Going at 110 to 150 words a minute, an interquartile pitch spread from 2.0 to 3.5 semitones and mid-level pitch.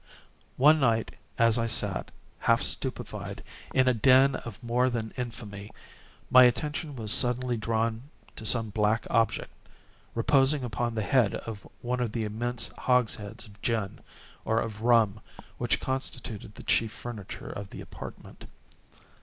No: average, 145 wpm; narrow, 2.5 semitones; low, 115 Hz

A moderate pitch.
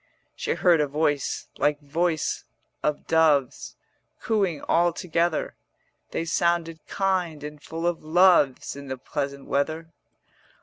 Yes: medium, 160 Hz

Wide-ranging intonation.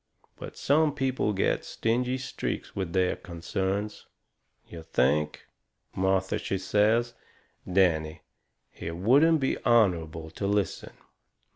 Yes: wide, 5.8 semitones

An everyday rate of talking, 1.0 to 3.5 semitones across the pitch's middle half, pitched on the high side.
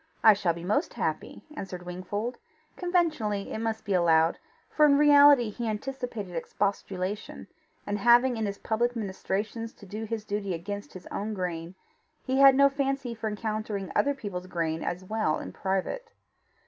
No: average, 160 wpm; average, 4.4 semitones; high, 210 Hz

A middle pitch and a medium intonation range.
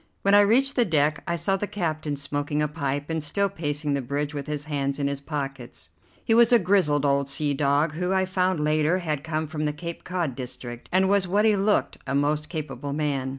Yes: medium, 150 Hz; average, 4.3 semitones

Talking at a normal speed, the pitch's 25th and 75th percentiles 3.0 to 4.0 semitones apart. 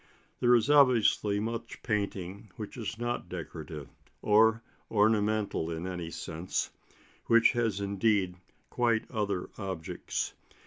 No: slow, 115 wpm; average, 3.7 semitones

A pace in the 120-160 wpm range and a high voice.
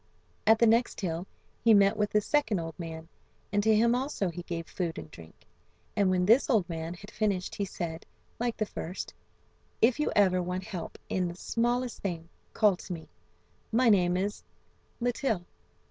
No: average, 180 wpm; high, 195 Hz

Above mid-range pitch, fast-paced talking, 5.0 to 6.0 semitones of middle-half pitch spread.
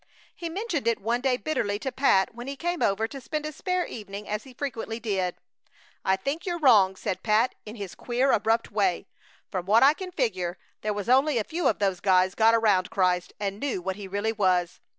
Yes: high, 225 Hz; fast, 215 wpm; wide, 5.5 semitones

